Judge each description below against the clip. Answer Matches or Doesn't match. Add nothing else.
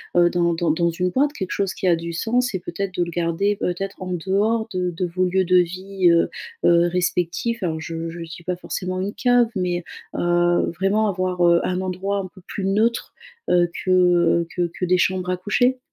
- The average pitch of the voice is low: Doesn't match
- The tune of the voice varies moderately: Doesn't match